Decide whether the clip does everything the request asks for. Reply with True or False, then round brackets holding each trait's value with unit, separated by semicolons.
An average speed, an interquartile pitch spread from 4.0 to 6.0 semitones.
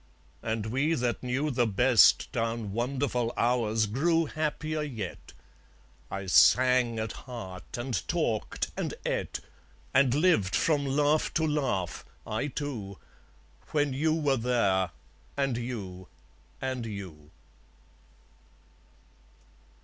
False (110 wpm; 4.6 semitones)